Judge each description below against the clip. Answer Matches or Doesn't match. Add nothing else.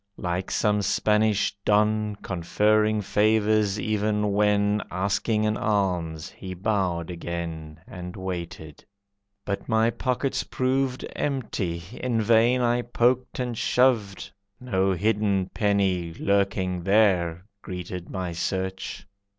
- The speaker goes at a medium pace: Doesn't match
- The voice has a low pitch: Matches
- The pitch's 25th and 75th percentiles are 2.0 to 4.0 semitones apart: Matches